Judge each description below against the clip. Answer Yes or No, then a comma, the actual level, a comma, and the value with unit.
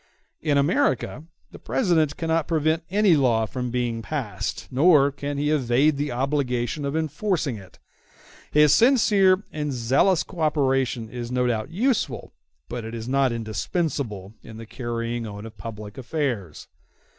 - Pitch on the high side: No, low, 135 Hz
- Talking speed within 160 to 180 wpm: No, average, 145 wpm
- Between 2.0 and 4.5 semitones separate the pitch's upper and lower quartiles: No, average, 5.1 semitones